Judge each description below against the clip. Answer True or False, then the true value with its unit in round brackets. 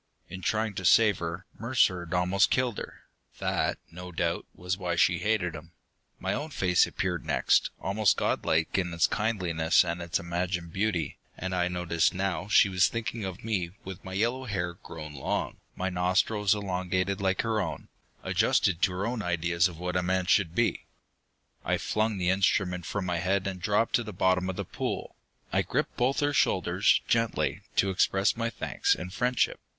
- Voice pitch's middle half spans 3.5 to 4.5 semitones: False (2.8 semitones)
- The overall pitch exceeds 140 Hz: False (95 Hz)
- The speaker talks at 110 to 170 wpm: False (185 wpm)